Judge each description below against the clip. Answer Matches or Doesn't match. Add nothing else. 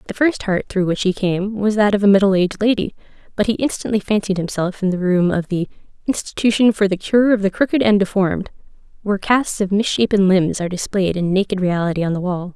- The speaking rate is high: Matches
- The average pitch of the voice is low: Doesn't match